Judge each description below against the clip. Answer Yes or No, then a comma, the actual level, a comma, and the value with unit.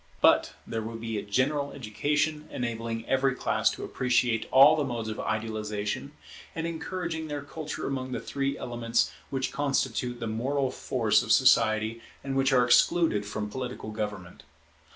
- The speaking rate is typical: Yes, average, 155 wpm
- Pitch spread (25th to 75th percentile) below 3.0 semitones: No, average, 3.8 semitones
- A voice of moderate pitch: No, low, 125 Hz